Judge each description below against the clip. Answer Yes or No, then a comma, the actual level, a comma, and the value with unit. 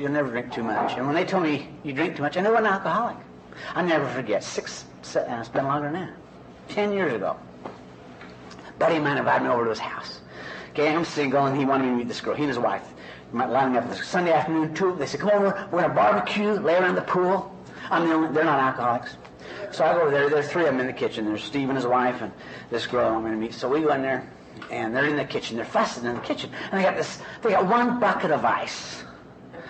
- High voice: No, low, 135 Hz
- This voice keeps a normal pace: No, fast, 260 wpm